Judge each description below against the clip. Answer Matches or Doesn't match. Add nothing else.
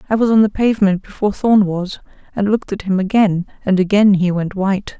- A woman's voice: Matches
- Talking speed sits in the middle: Doesn't match